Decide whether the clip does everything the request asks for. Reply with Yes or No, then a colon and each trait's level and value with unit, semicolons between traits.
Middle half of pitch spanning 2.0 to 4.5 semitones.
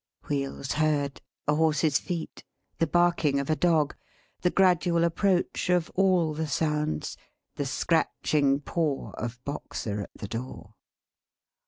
Yes: average, 3.4 semitones